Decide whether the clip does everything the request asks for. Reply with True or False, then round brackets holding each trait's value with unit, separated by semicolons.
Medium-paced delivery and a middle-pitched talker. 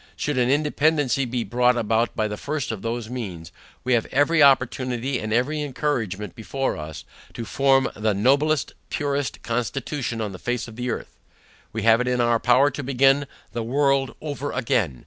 False (180 wpm; 125 Hz)